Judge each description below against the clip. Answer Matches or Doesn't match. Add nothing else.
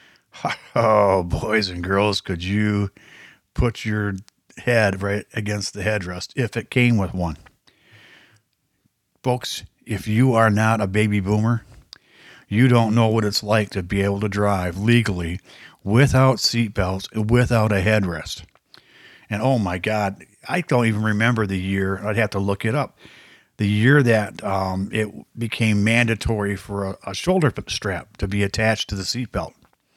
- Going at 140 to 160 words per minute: Matches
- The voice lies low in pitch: Matches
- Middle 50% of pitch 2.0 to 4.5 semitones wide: Matches